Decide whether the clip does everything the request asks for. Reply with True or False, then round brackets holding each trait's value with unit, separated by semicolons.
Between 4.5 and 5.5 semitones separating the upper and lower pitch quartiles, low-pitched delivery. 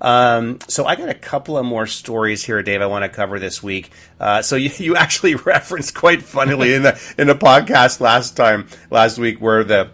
True (5.0 semitones; 115 Hz)